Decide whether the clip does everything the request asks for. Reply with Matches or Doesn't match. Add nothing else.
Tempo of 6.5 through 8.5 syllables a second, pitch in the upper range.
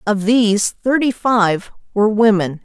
Doesn't match